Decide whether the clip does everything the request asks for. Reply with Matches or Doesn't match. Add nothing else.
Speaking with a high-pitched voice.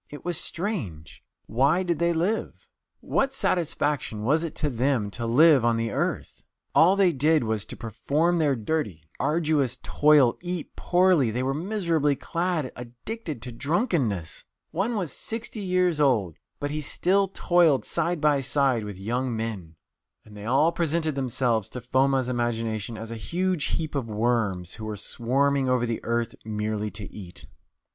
Doesn't match